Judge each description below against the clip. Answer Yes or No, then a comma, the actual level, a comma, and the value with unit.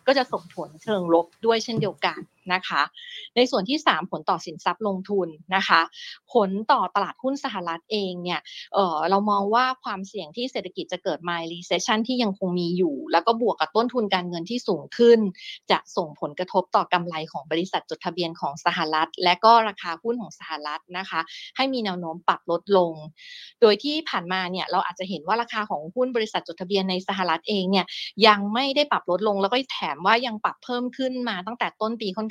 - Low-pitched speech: No, high, 195 Hz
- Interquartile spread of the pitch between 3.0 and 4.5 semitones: No, average, 4.9 semitones